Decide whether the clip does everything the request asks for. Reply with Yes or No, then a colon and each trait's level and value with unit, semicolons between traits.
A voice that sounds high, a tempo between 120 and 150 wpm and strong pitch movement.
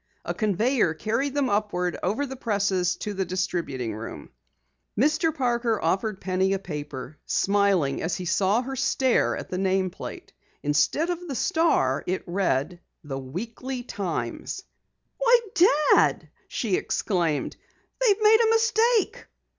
Yes: high, 205 Hz; slow, 135 wpm; wide, 7.3 semitones